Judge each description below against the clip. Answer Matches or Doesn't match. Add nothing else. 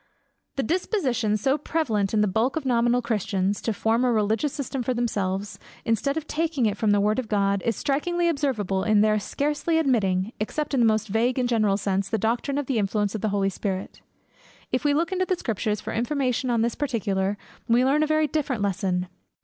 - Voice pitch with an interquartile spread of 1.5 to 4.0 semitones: Doesn't match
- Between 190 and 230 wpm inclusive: Matches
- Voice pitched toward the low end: Doesn't match